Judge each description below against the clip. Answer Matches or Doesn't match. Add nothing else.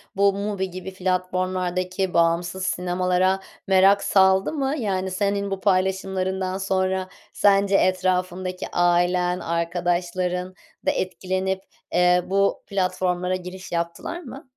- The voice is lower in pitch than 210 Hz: Matches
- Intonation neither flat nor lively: Doesn't match